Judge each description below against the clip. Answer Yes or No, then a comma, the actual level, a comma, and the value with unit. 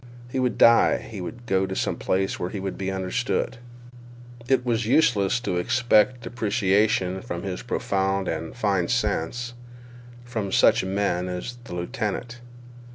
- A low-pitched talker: Yes, low, 100 Hz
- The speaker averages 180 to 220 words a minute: No, average, 150 wpm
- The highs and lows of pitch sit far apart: No, average, 4.3 semitones